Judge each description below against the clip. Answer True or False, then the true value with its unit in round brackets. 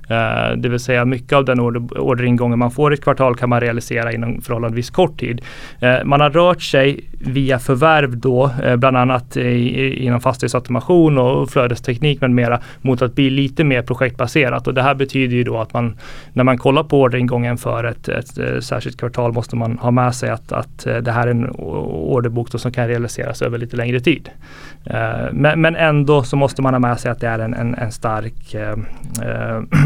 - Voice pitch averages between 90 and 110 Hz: False (125 Hz)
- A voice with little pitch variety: True (2.2 semitones)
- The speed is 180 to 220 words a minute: True (190 wpm)